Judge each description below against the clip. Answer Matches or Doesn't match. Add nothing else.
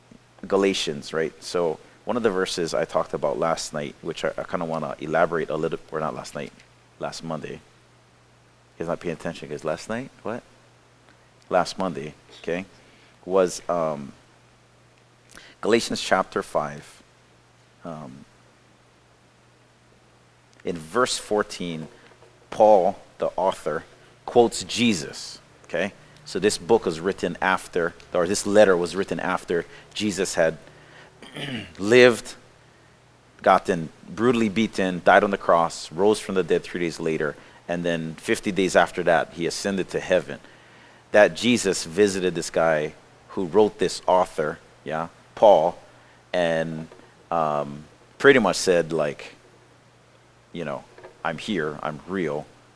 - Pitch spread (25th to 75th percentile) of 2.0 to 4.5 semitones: Doesn't match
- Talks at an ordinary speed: Doesn't match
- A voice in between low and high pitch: Doesn't match